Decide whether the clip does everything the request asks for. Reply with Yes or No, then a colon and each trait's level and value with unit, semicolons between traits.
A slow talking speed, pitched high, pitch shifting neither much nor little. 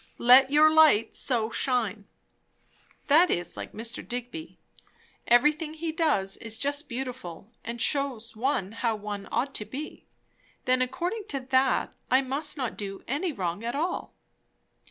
No: average, 145 wpm; very high, 255 Hz; average, 4.7 semitones